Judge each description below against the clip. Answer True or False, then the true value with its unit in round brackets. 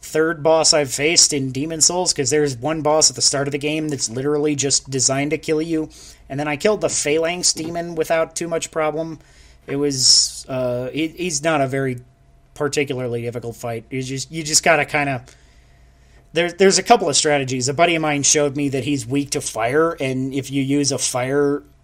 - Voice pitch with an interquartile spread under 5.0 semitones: True (3.0 semitones)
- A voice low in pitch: False (145 Hz)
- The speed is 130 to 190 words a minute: False (205 wpm)